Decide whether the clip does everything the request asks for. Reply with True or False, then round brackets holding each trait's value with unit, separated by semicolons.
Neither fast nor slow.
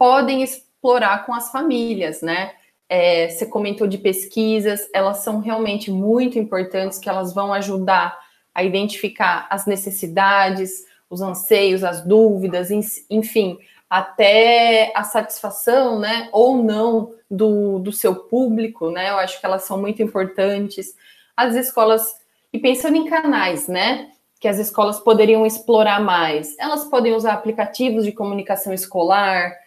True (135 wpm)